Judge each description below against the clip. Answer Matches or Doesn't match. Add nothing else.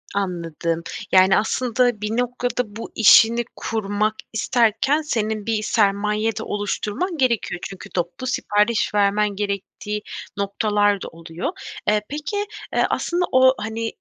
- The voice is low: Doesn't match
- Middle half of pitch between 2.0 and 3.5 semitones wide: Matches